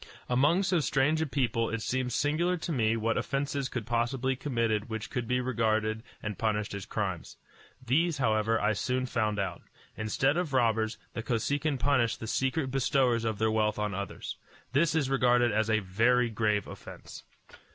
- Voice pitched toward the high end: No, low, 120 Hz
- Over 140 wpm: Yes, average, 175 wpm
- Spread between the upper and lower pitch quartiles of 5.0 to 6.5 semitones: No, average, 3.7 semitones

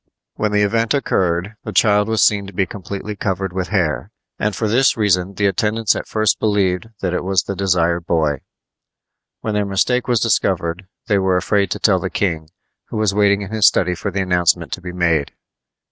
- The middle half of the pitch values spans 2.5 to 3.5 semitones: Yes, average, 2.8 semitones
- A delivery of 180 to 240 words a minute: Yes, average, 200 wpm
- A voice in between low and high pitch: No, low, 100 Hz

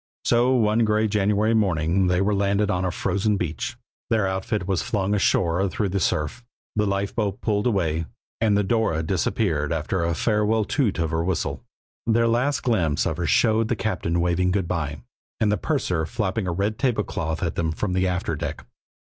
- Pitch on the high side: No, low, 100 Hz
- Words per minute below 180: No, average, 185 wpm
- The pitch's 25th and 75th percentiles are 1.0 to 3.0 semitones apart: No, average, 4.1 semitones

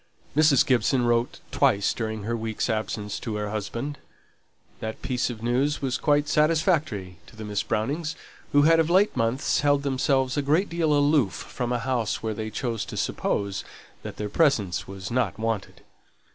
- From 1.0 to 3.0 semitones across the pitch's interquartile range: No, average, 5.0 semitones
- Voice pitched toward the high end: No, low, 120 Hz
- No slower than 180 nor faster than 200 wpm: No, average, 170 wpm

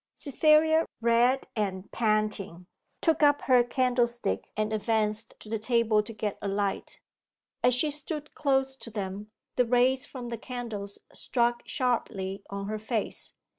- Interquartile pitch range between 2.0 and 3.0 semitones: No, average, 3.4 semitones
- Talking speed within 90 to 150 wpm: Yes, average, 145 wpm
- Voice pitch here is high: Yes, high, 235 Hz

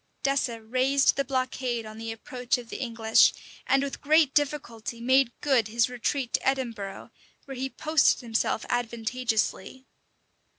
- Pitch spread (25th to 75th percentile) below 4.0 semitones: Yes, average, 2.9 semitones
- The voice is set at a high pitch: Yes, very high, 250 Hz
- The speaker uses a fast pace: No, average, 145 wpm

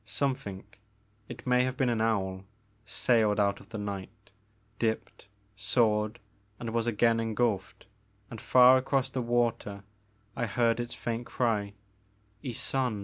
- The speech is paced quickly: No, average, 145 wpm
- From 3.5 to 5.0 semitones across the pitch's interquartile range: No, average, 2.8 semitones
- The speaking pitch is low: Yes, low, 115 Hz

